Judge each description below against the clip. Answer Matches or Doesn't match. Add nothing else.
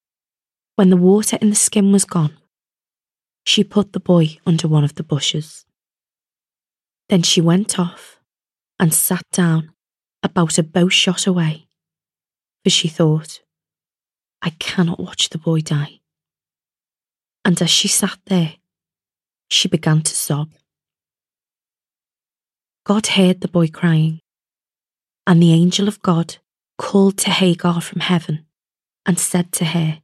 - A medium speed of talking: Doesn't match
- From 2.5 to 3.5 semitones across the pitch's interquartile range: Matches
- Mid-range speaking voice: Matches